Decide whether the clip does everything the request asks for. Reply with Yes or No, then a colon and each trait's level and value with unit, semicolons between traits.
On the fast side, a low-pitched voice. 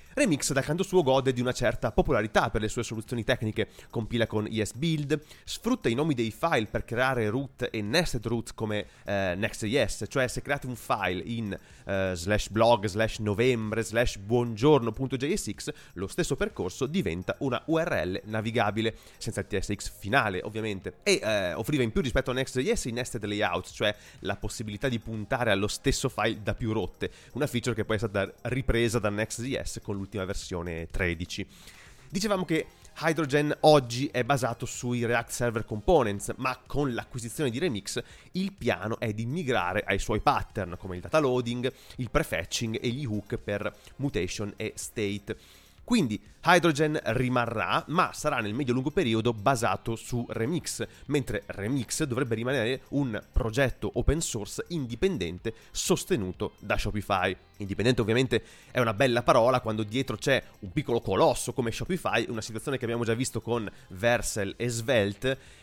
No: average, 160 wpm; low, 115 Hz